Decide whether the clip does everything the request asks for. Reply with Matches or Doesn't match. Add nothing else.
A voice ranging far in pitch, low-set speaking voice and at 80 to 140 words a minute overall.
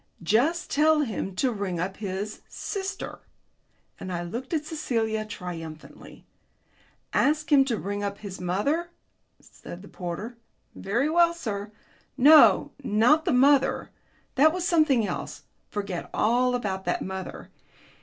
Doesn't match